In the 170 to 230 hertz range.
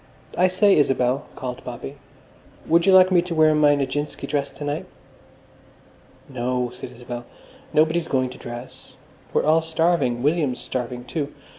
No: medium, 145 Hz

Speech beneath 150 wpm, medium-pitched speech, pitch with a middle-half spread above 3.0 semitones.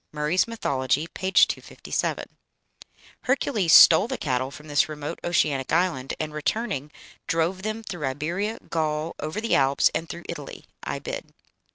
Yes: average, 140 wpm; medium, 160 Hz; average, 4.3 semitones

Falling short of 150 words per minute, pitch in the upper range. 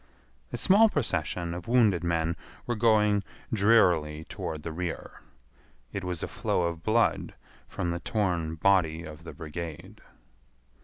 No: average, 140 wpm; very low, 85 Hz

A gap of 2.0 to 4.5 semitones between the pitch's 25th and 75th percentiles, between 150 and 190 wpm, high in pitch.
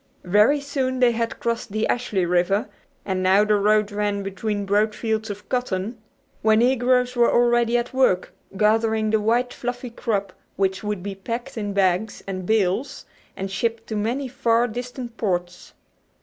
Yes: average, 3.2 semitones; average, 165 wpm; high, 220 Hz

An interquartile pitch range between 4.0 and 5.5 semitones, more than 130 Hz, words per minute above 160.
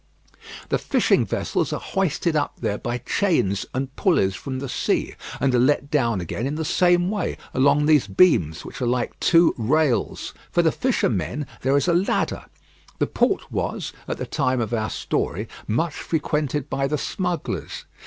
Yes: average, 5.1 semitones; medium, 140 Hz; average, 175 wpm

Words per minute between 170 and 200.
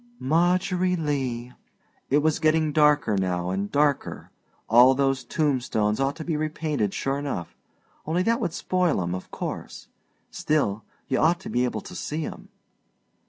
No: average, 155 wpm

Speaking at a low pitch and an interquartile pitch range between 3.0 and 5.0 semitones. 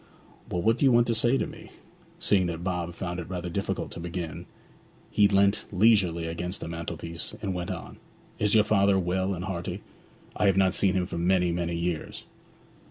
No: very low, 90 Hz; narrow, 2.5 semitones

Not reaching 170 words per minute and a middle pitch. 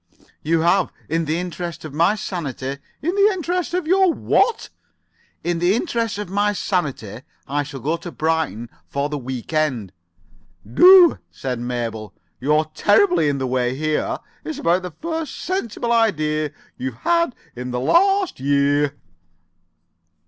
Yes: average, 150 wpm; medium, 160 Hz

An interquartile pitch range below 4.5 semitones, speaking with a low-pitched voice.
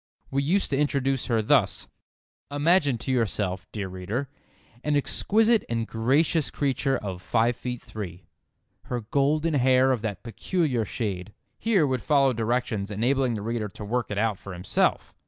No: average, 4.8 semitones; low, 125 Hz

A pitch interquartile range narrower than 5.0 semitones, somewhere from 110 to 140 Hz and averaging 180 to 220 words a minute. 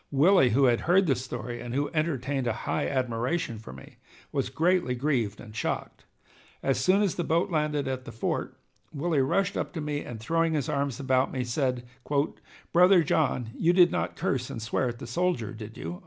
No: wide, 5.4 semitones; low, 135 Hz; average, 200 wpm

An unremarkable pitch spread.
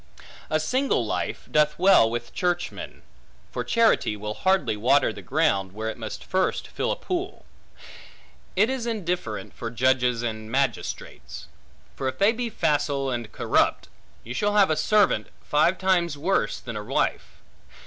No: wide, 8.6 semitones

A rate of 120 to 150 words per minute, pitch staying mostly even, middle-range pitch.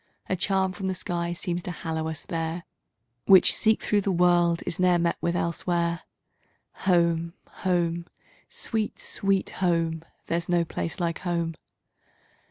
Yes: average, 145 wpm; narrow, 1.5 semitones; medium, 175 Hz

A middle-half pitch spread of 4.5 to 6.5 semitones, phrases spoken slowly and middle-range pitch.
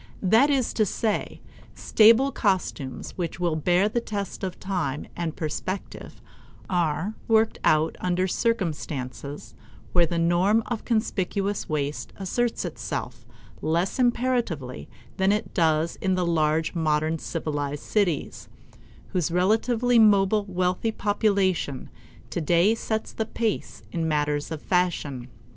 Yes: average, 5.2 semitones; slow, 120 wpm; medium, 180 Hz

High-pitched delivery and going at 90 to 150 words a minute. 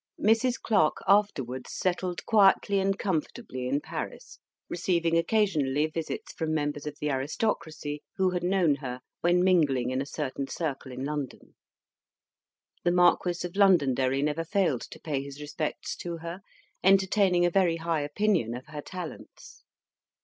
No: medium, 165 Hz; average, 145 wpm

